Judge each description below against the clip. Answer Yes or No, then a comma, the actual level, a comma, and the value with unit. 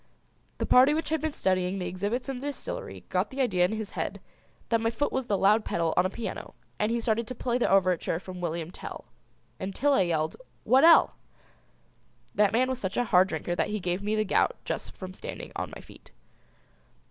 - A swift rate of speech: Yes, fast, 210 wpm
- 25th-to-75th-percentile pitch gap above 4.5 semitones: Yes, wide, 5.4 semitones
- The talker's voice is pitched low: No, high, 210 Hz